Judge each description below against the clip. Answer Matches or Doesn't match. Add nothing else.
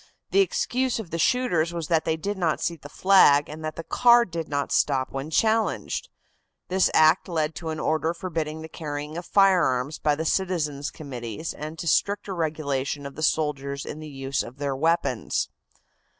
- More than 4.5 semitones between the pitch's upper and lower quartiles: Doesn't match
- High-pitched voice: Doesn't match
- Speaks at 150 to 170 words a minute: Doesn't match